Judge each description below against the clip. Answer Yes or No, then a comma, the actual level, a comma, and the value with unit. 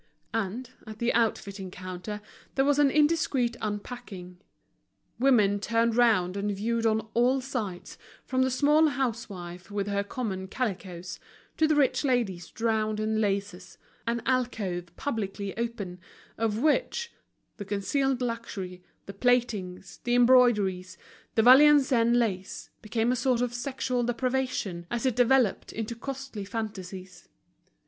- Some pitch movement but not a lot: Yes, average, 4.2 semitones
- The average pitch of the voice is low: No, high, 225 Hz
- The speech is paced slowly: Yes, slow, 130 wpm